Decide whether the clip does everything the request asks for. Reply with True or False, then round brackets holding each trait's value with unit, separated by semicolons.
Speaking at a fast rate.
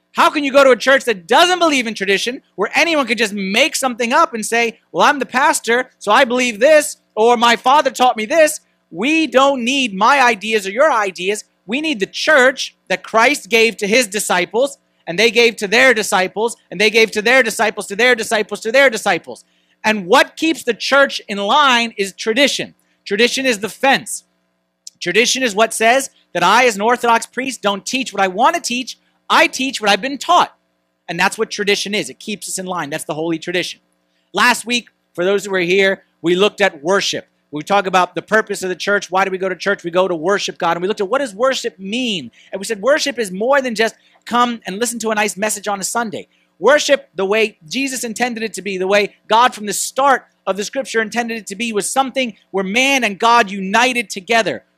True (225 wpm)